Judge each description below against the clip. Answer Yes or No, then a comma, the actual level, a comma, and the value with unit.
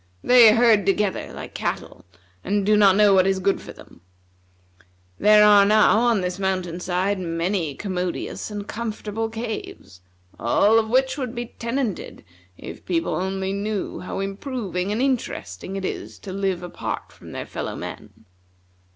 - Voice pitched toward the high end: Yes, high, 205 Hz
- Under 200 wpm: Yes, average, 155 wpm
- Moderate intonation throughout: Yes, average, 3.0 semitones